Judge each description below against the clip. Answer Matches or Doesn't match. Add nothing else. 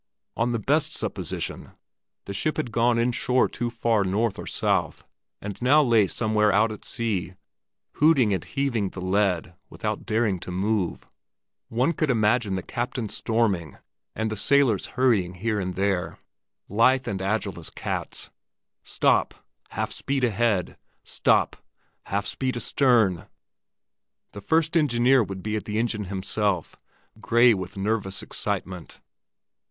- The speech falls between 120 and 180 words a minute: Matches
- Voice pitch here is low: Matches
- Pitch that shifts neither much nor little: Matches